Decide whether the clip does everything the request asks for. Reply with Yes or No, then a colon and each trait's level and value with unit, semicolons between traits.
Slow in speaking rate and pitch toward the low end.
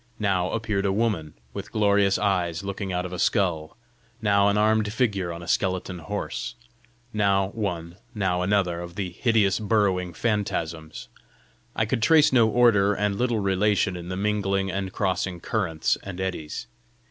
No: average, 160 wpm; low, 100 Hz